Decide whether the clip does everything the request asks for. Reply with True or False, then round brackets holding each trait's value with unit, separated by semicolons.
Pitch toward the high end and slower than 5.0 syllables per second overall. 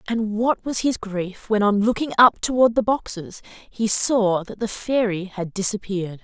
True (210 Hz; 4.4 syllables/s)